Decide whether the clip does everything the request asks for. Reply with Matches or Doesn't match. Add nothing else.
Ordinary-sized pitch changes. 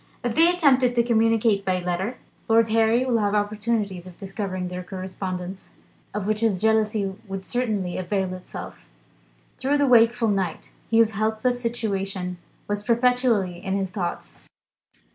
Matches